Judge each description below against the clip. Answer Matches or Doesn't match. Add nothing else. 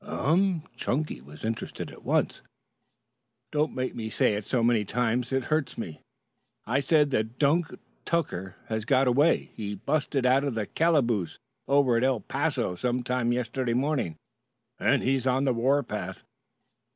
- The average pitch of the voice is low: Matches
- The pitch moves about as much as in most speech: Matches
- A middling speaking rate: Matches